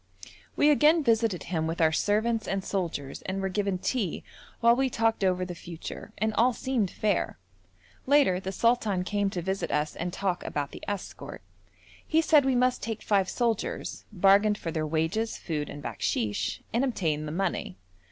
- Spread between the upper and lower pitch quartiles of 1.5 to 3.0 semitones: No, average, 4.9 semitones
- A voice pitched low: No, high, 195 Hz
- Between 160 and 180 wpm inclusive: Yes, average, 175 wpm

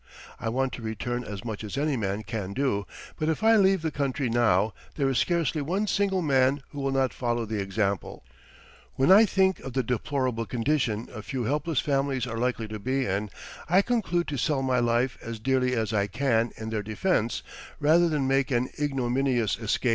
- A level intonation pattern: No, average, 4.4 semitones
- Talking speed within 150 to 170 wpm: No, average, 200 wpm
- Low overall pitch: Yes, low, 130 Hz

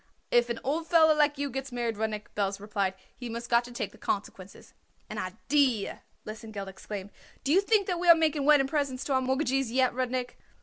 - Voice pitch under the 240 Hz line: No, very high, 255 Hz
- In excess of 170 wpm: Yes, fast, 205 wpm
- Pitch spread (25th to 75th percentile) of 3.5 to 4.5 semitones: No, average, 5.0 semitones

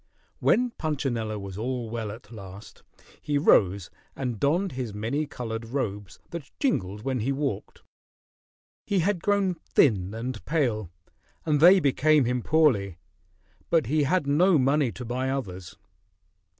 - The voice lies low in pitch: Yes, low, 130 Hz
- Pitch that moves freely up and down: Yes, wide, 5.9 semitones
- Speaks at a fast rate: No, average, 140 wpm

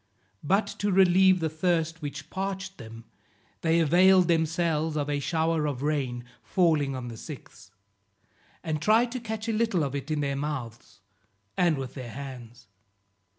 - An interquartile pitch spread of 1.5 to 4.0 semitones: No, average, 4.7 semitones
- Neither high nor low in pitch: Yes, medium, 155 Hz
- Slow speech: No, average, 155 wpm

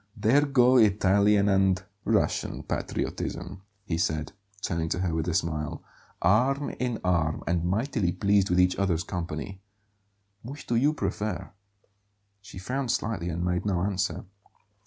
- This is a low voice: Yes, very low, 95 Hz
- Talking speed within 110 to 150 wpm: Yes, average, 140 wpm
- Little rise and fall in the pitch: No, average, 4.0 semitones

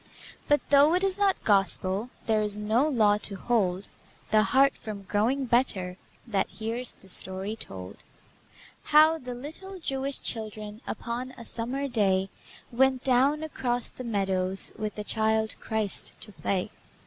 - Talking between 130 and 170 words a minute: Yes, average, 150 wpm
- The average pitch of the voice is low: No, high, 225 Hz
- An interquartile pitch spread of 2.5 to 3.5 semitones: No, average, 4.4 semitones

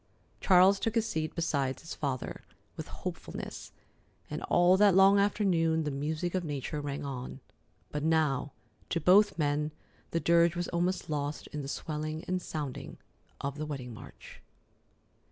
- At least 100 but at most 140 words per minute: No, average, 155 wpm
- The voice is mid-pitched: Yes, medium, 160 Hz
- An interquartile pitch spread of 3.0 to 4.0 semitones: Yes, average, 3.7 semitones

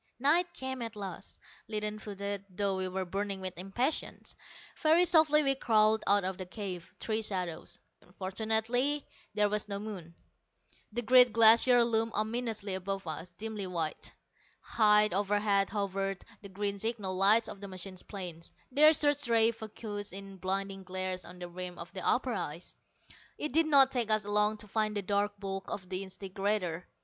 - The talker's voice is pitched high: Yes, high, 205 Hz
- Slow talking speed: No, average, 165 wpm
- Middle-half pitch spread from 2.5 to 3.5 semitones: Yes, average, 2.8 semitones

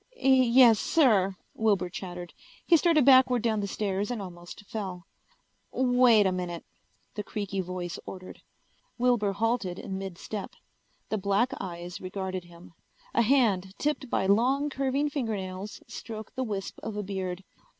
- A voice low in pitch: No, high, 205 Hz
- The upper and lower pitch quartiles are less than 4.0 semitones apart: No, average, 4.9 semitones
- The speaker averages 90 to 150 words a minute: Yes, average, 145 wpm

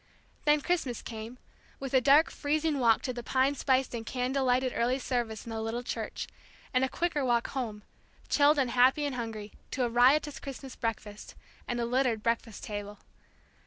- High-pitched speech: Yes, very high, 250 Hz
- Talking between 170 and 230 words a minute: Yes, average, 180 wpm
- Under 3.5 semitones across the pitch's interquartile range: Yes, average, 2.9 semitones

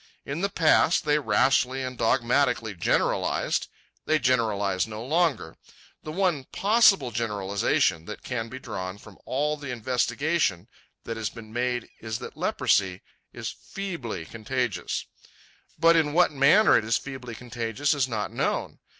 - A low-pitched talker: Yes, low, 125 Hz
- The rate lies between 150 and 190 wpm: No, average, 140 wpm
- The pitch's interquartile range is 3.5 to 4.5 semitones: No, average, 5.1 semitones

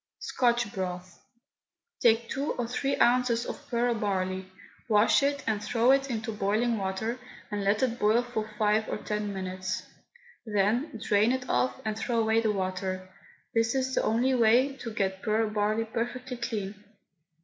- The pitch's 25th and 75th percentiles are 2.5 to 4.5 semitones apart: Yes, average, 3.0 semitones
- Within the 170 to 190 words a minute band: No, average, 160 wpm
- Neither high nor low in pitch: No, high, 220 Hz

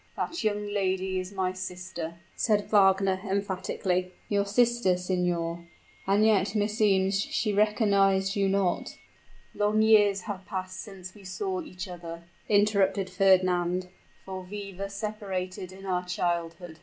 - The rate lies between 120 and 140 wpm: Yes, slow, 135 wpm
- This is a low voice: No, high, 190 Hz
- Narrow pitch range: Yes, narrow, 2.0 semitones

